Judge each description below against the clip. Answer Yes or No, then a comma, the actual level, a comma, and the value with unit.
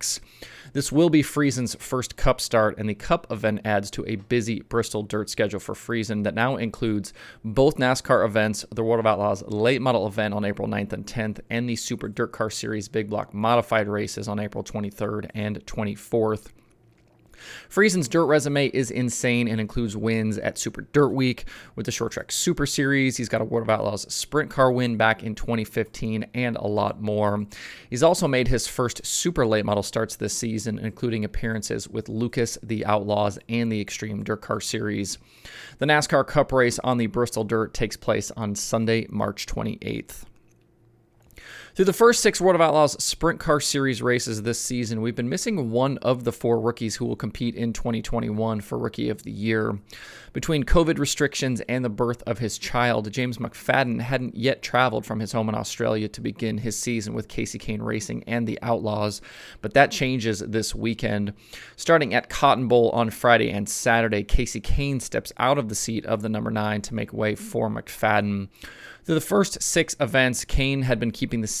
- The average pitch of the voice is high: No, low, 115 Hz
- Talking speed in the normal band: Yes, average, 190 wpm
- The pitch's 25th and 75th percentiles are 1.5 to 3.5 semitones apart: Yes, average, 2.9 semitones